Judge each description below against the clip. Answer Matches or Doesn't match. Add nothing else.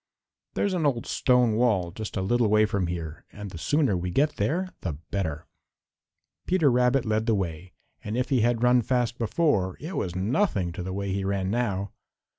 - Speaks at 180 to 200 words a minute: Matches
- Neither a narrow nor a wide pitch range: Matches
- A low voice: Matches